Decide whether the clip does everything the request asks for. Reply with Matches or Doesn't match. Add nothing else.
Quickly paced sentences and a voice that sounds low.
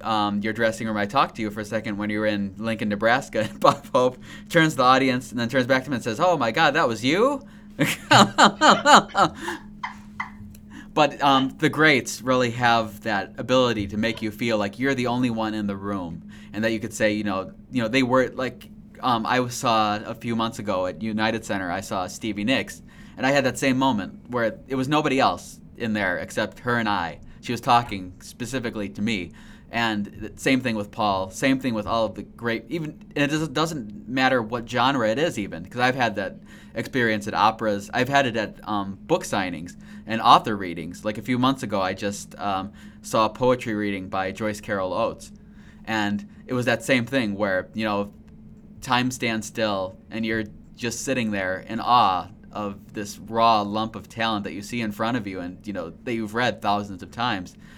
Matches